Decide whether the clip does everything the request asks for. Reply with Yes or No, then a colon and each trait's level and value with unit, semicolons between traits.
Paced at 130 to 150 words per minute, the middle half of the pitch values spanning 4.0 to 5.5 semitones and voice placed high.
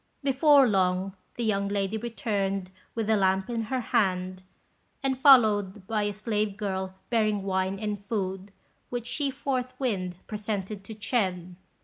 No: average, 140 wpm; average, 3.4 semitones; high, 205 Hz